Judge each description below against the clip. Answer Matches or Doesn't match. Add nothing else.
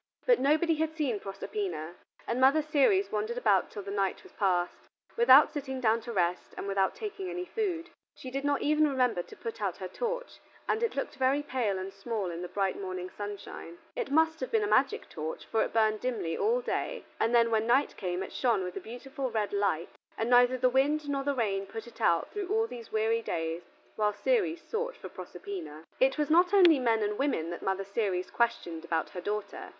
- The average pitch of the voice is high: Matches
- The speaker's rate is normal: Doesn't match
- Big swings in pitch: Matches